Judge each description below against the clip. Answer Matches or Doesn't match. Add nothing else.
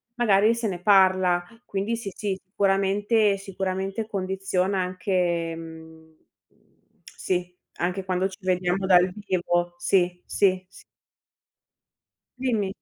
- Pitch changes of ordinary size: Doesn't match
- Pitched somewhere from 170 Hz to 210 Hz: Matches